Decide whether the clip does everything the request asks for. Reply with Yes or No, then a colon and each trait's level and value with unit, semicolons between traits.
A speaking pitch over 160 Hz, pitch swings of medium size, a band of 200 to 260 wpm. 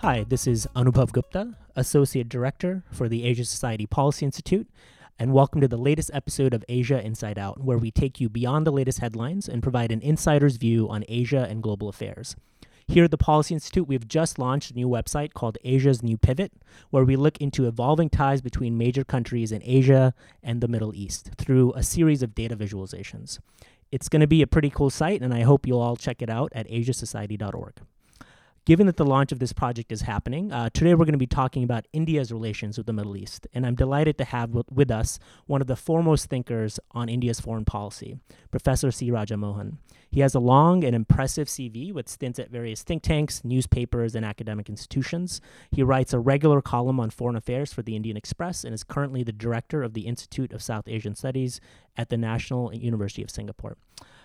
No: low, 125 Hz; average, 3.4 semitones; fast, 205 wpm